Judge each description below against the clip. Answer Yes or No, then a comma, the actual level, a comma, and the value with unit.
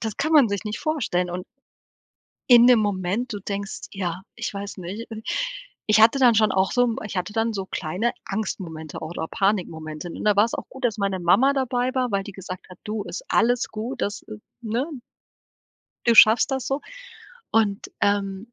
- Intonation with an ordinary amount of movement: Yes, average, 3.7 semitones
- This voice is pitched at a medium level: No, high, 210 Hz